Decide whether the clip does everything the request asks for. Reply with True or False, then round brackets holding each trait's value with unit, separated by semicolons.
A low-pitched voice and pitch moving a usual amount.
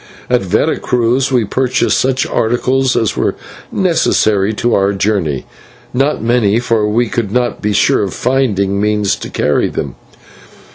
True (115 Hz; 3.7 semitones)